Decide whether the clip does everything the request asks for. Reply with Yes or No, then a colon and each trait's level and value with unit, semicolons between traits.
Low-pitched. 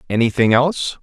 Yes: low, 125 Hz